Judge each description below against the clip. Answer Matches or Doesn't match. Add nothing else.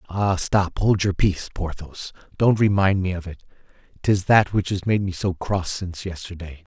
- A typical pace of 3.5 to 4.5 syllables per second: Doesn't match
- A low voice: Matches